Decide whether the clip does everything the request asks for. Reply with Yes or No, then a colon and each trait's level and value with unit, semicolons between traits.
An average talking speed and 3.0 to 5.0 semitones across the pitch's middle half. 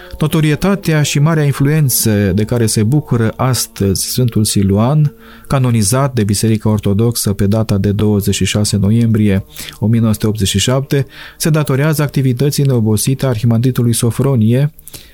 No: slow, 110 wpm; average, 4.6 semitones